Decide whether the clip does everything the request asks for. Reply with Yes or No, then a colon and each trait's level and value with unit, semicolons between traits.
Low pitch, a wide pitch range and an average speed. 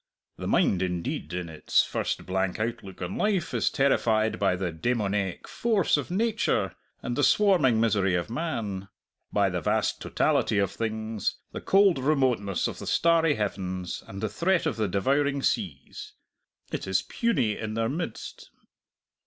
Yes: low, 110 Hz; wide, 7.0 semitones; average, 155 wpm